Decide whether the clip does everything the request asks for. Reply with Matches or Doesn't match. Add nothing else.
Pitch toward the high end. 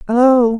Matches